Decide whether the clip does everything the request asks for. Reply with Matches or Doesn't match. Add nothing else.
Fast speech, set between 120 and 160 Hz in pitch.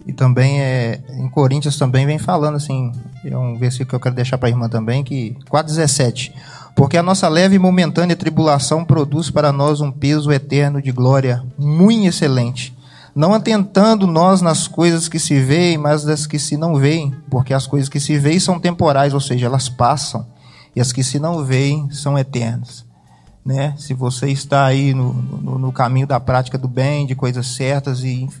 Matches